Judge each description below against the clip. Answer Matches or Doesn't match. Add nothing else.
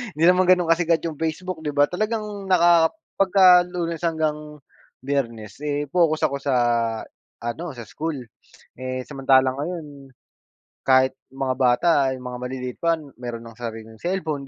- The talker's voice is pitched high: Doesn't match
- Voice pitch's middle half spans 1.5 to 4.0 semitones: Doesn't match